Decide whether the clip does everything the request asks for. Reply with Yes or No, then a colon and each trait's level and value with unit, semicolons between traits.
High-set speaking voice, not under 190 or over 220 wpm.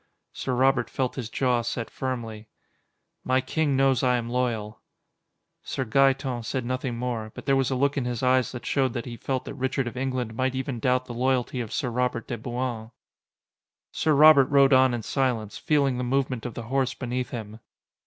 No: low, 125 Hz; average, 195 wpm